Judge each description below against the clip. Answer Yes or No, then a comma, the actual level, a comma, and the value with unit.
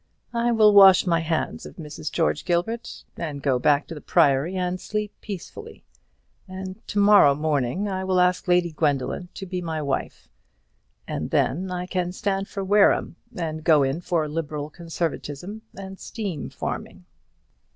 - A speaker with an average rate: Yes, average, 160 wpm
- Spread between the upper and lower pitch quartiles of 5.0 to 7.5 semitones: No, average, 3.8 semitones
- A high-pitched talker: No, medium, 175 Hz